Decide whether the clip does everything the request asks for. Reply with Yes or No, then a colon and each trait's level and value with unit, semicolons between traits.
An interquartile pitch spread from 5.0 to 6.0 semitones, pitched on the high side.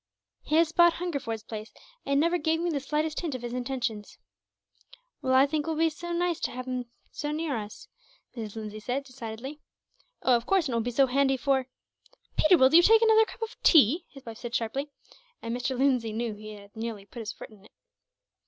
Yes: wide, 5.6 semitones; very high, 265 Hz